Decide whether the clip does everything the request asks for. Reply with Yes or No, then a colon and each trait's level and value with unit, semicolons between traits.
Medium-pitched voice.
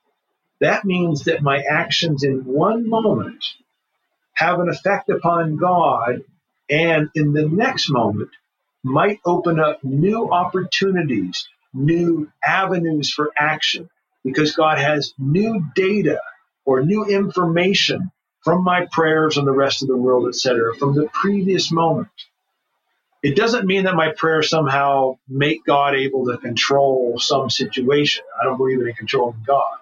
Yes: medium, 155 Hz